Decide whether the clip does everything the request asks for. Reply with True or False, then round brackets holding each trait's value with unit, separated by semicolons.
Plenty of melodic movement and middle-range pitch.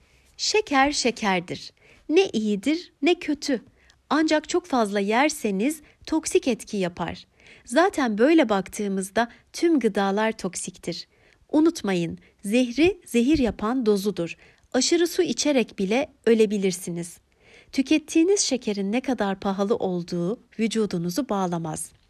False (7.1 semitones; 230 Hz)